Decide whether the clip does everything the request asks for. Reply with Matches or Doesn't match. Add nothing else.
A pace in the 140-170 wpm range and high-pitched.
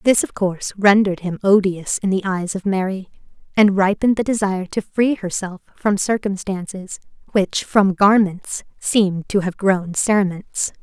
Matches